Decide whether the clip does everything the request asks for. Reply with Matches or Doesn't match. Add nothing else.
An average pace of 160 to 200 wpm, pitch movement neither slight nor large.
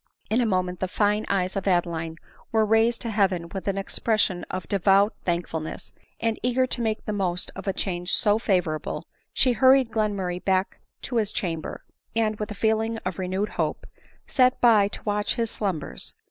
Matches